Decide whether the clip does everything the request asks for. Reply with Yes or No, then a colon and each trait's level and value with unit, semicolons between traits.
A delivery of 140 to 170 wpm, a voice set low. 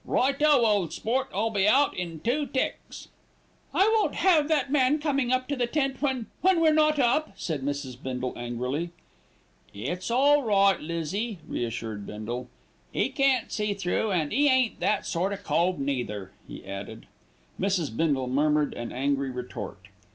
No: average, 160 wpm; high, 195 Hz